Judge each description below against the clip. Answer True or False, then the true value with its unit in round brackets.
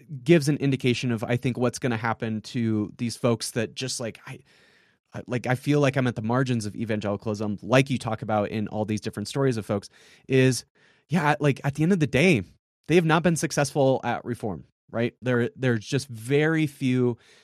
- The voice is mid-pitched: False (125 Hz)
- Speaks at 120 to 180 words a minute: False (205 wpm)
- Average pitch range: True (3.7 semitones)